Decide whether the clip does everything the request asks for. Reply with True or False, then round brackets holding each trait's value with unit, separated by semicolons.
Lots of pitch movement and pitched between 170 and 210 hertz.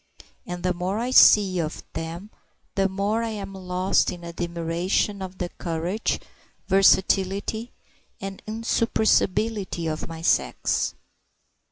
False (2.9 semitones; 190 Hz)